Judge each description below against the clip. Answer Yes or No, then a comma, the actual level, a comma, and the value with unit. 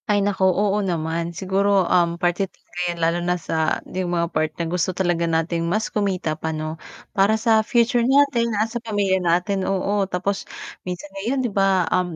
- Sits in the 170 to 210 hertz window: Yes, medium, 185 Hz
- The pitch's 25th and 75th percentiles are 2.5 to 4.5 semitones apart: Yes, average, 3.1 semitones